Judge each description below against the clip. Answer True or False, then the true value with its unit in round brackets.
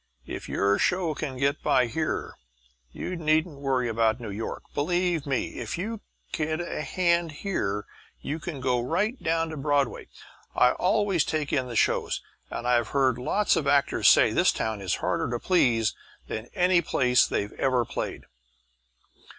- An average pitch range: False (5.8 semitones)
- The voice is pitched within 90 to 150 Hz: True (140 Hz)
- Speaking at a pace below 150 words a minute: False (165 wpm)